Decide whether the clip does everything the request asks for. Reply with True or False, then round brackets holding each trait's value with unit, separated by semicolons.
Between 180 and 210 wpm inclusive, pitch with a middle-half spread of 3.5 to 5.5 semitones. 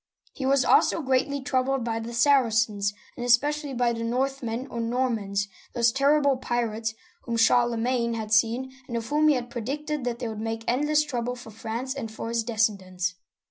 False (185 wpm; 2.9 semitones)